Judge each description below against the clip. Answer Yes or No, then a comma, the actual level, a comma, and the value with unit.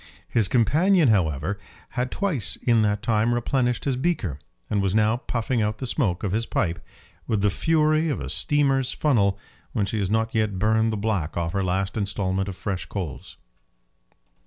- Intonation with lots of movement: No, average, 4.2 semitones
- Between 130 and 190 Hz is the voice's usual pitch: No, low, 110 Hz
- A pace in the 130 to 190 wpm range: Yes, average, 180 wpm